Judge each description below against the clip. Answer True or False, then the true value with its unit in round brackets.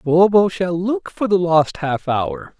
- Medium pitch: True (175 Hz)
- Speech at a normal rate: True (185 wpm)